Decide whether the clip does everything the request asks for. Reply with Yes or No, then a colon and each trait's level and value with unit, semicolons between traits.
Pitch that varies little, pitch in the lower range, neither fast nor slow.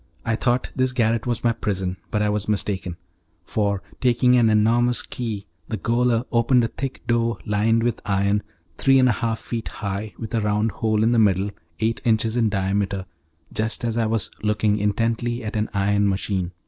Yes: narrow, 2.3 semitones; low, 110 Hz; average, 185 wpm